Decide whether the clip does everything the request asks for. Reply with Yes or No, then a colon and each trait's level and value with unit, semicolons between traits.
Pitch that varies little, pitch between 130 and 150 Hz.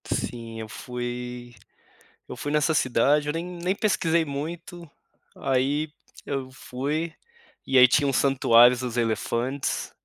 No: average, 3.8 semitones; low, 135 Hz